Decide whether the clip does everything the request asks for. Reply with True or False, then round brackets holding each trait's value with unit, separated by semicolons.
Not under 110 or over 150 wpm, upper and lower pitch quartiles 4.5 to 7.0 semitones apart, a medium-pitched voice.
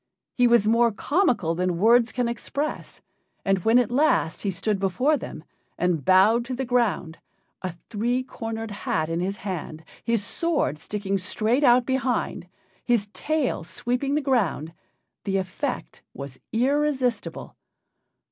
False (140 wpm; 5.0 semitones; 225 Hz)